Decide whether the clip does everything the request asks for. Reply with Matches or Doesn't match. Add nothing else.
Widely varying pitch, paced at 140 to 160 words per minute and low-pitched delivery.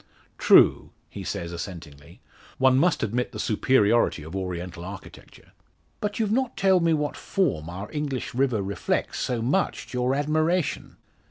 Matches